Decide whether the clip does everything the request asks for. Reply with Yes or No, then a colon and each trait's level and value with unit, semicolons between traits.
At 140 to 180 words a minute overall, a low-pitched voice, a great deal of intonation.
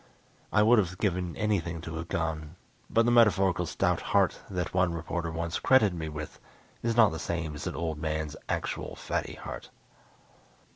No: average, 175 wpm; very low, 85 Hz; average, 3.8 semitones